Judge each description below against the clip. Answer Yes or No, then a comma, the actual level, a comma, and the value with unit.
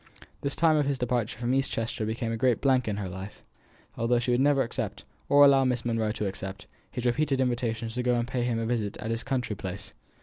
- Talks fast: Yes, fast, 235 wpm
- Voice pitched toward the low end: Yes, low, 120 Hz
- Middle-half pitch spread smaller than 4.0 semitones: Yes, average, 2.7 semitones